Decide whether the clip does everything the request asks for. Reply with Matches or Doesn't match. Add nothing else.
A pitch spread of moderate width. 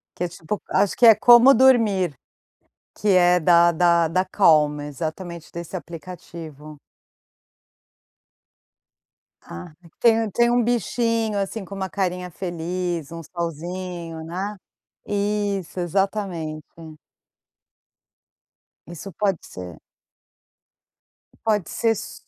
Matches